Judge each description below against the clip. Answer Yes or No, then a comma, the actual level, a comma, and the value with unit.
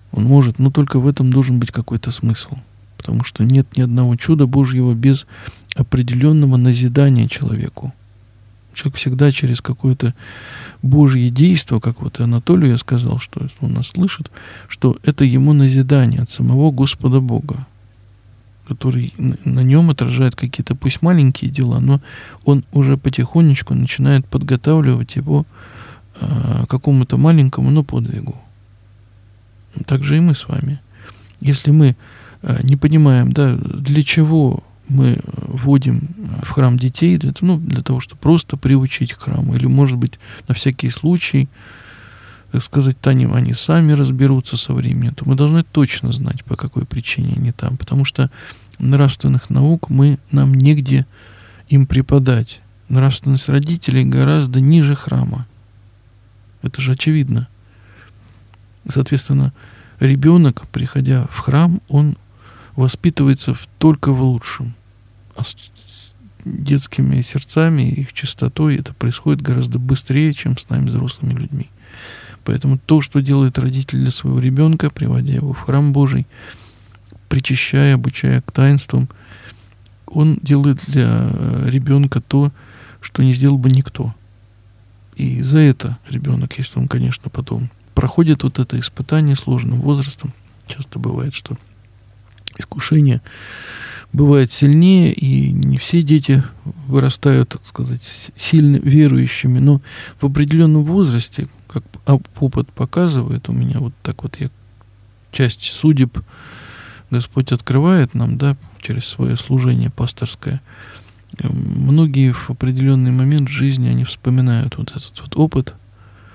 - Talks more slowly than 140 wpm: Yes, average, 125 wpm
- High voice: No, low, 130 Hz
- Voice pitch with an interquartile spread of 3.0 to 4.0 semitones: Yes, average, 3.7 semitones